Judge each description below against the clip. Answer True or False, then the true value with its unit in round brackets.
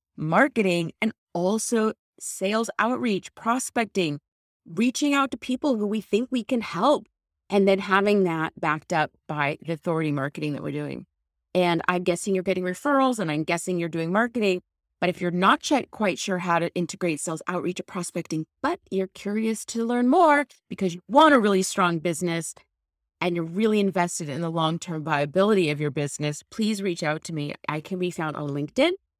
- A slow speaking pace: False (185 wpm)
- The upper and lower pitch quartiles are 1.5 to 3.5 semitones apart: False (5.1 semitones)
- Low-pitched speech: False (180 Hz)